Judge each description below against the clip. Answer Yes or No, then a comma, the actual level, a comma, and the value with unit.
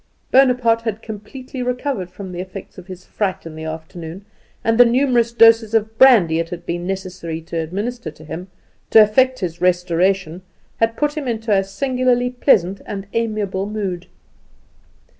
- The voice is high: Yes, high, 205 Hz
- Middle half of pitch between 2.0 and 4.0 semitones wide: No, average, 4.9 semitones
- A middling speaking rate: Yes, average, 165 wpm